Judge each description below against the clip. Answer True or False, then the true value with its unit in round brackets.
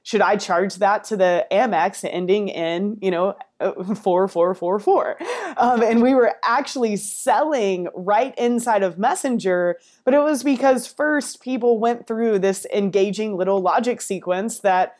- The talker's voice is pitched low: False (205 Hz)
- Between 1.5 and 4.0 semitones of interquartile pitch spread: False (4.5 semitones)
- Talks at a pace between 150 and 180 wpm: True (160 wpm)